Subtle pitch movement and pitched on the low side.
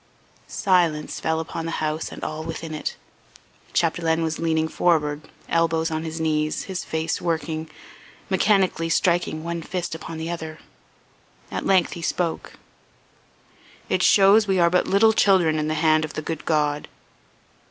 No: narrow, 1.7 semitones; medium, 165 Hz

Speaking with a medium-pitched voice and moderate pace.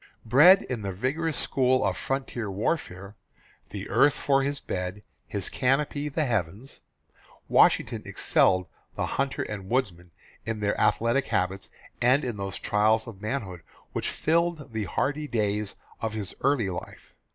No: low, 115 Hz; average, 145 wpm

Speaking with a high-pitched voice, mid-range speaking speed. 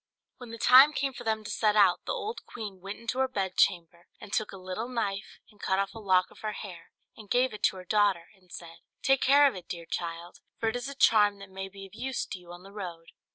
No: high, 205 Hz; fast, 265 wpm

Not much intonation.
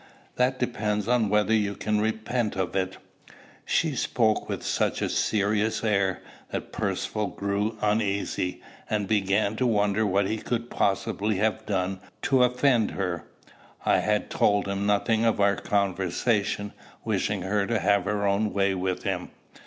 Yes: narrow, 1.9 semitones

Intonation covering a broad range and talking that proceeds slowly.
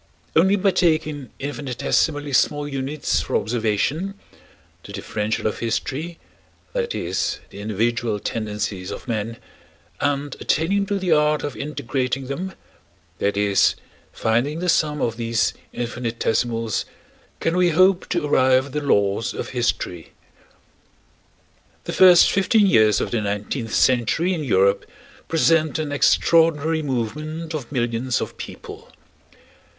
Yes: wide, 5.8 semitones; slow, 125 wpm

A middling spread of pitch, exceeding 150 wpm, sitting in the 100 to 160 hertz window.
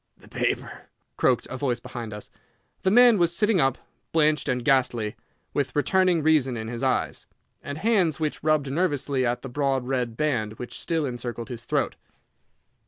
Yes: average, 4.4 semitones; average, 170 wpm; low, 135 Hz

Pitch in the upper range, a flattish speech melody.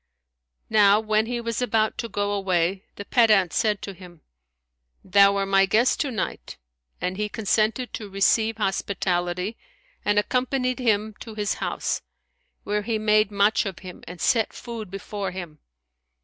Yes: high, 205 Hz; narrow, 2.3 semitones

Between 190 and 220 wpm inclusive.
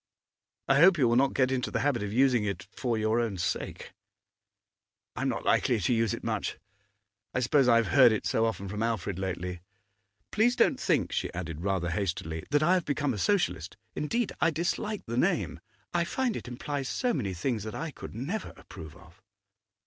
Yes: average, 200 wpm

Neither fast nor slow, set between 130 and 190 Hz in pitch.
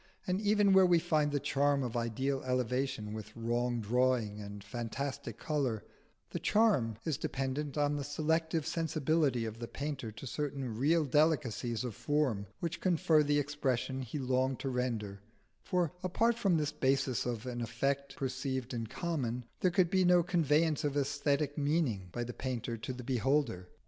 Yes: average, 165 wpm; low, 135 Hz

